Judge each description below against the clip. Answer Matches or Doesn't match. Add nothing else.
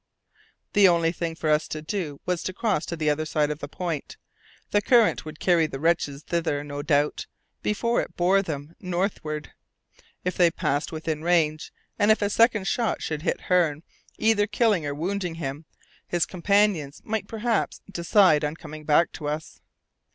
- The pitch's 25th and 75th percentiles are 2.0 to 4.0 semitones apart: Doesn't match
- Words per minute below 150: Doesn't match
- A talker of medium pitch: Matches